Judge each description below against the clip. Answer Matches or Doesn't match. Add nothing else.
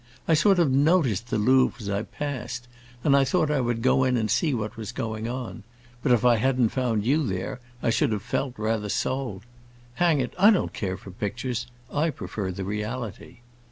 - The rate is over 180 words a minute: Matches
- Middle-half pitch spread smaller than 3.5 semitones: Doesn't match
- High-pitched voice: Doesn't match